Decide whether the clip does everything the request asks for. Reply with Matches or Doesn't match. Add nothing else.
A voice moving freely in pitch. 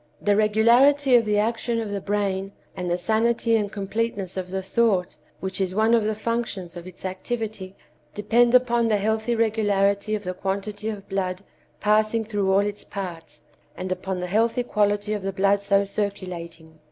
Doesn't match